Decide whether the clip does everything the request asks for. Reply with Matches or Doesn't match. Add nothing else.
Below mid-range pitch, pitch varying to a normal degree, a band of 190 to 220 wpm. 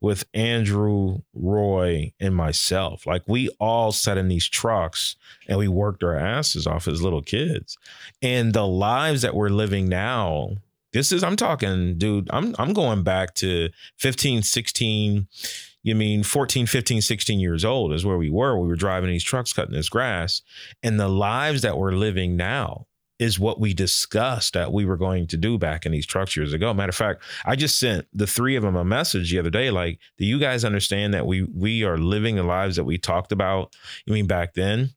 Matches